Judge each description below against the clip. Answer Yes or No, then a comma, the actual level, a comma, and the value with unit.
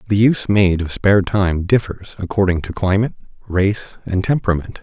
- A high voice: No, very low, 95 Hz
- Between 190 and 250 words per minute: No, average, 160 wpm